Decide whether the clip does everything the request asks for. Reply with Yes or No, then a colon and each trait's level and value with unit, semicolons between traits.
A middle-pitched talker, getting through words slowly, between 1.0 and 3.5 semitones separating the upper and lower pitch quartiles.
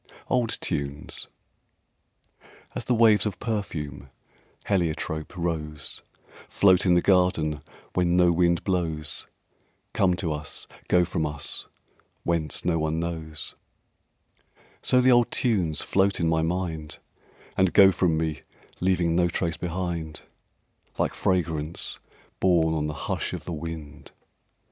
No: very low, 85 Hz; slow, 125 wpm; average, 2.8 semitones